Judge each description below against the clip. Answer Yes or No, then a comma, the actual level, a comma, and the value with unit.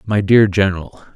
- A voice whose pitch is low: Yes, low, 100 Hz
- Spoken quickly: No, average, 155 wpm